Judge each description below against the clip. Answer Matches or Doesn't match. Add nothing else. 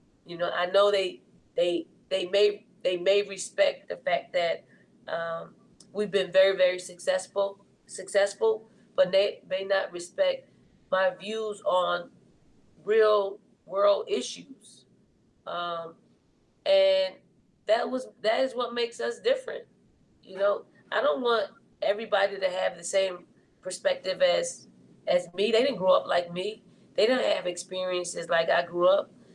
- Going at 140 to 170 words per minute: Matches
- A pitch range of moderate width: Matches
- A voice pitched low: Doesn't match